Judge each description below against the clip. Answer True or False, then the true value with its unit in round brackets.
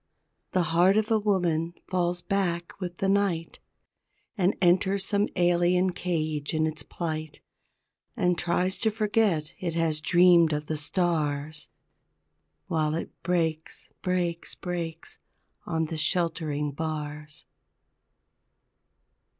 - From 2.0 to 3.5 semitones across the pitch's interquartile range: True (2.5 semitones)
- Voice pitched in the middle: True (170 Hz)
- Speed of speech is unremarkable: False (115 wpm)